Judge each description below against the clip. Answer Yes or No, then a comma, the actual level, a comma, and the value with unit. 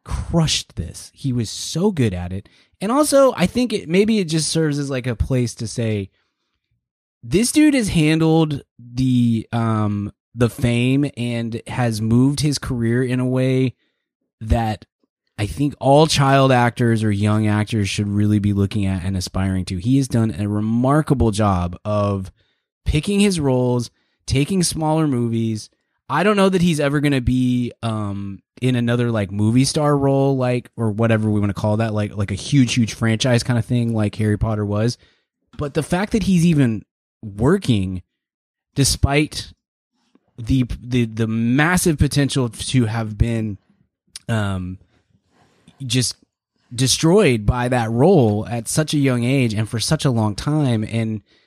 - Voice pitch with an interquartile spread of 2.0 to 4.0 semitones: No, average, 4.7 semitones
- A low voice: Yes, low, 120 Hz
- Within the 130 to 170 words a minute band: Yes, average, 160 wpm